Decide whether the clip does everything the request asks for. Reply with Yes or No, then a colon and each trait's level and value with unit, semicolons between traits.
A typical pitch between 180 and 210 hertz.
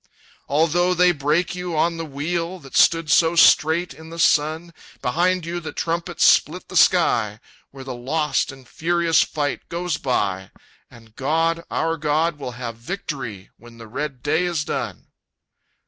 No: medium, 160 Hz